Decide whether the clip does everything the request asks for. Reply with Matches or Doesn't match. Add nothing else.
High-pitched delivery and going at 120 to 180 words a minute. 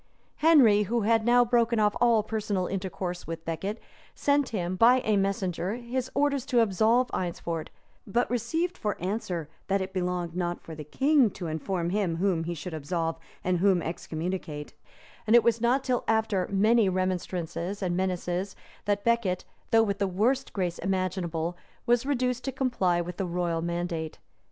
Matches